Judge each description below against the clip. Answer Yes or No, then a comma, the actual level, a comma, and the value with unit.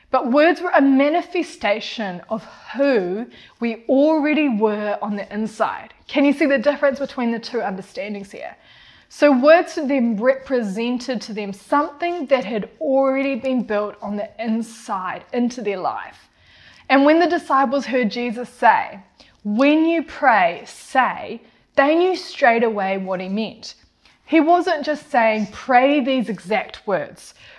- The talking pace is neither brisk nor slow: Yes, average, 150 wpm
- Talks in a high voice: Yes, very high, 255 Hz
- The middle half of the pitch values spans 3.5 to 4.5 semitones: No, average, 5.1 semitones